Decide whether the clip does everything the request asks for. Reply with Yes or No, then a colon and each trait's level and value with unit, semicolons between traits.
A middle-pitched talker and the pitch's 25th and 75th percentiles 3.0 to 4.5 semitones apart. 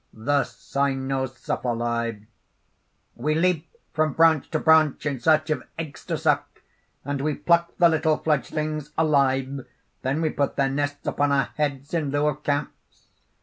No: medium, 145 Hz; narrow, 2.4 semitones